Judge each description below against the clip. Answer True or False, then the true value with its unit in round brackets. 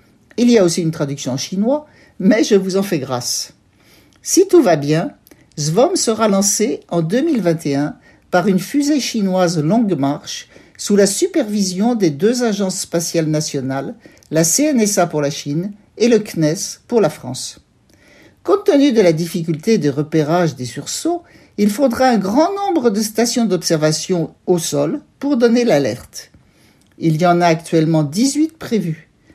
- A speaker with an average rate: True (155 wpm)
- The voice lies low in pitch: False (185 Hz)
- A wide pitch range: True (6.9 semitones)